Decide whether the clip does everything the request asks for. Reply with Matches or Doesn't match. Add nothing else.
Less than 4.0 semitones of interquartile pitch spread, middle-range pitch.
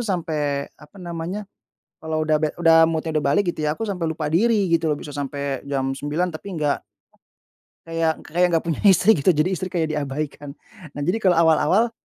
Matches